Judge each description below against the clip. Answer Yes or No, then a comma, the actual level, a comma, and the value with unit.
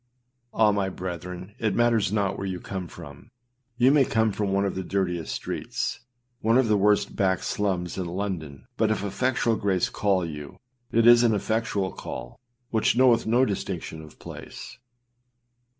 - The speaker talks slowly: No, average, 165 wpm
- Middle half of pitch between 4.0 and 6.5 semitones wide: No, average, 3.5 semitones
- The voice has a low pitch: Yes, low, 100 Hz